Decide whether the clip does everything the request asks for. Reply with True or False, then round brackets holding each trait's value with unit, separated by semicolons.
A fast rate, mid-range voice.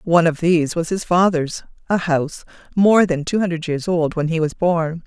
True (215 wpm; 170 Hz)